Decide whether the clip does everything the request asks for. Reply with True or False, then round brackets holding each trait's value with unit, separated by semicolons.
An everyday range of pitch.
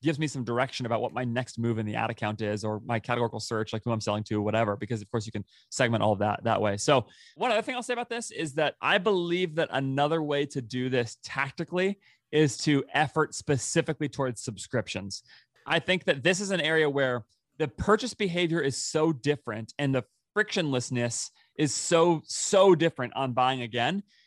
False (6.0 semitones)